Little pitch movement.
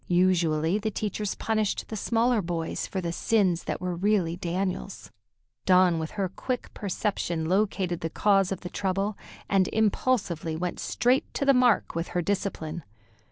No: average, 3.5 semitones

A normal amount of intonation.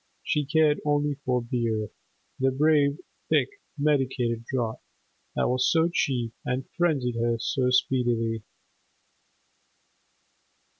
Yes: average, 3.7 semitones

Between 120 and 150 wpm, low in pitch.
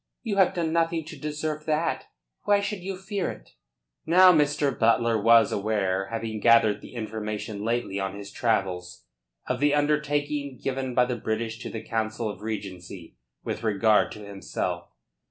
No: average, 160 wpm; low, 115 Hz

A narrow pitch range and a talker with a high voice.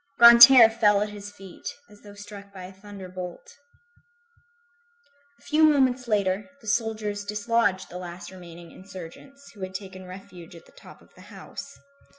No: average, 3.4 semitones; high, 205 Hz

